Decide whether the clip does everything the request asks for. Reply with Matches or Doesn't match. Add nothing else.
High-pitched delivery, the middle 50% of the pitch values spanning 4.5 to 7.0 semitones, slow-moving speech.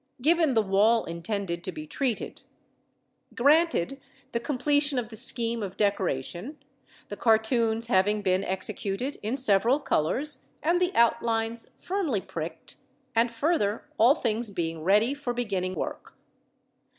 Matches